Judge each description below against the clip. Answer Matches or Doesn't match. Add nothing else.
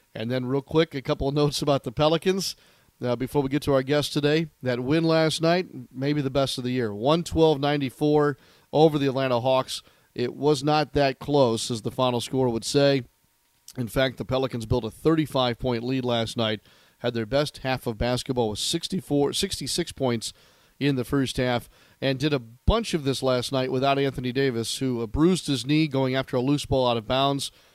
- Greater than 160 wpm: Matches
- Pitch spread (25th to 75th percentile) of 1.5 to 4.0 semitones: Matches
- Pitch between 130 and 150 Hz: Matches